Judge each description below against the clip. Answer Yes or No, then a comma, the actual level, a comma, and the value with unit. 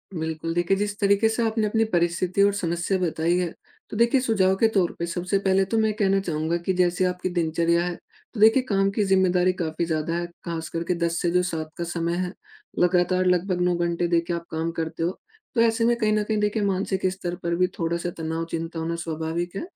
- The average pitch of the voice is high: No, medium, 180 Hz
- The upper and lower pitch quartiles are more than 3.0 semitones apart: No, average, 2.7 semitones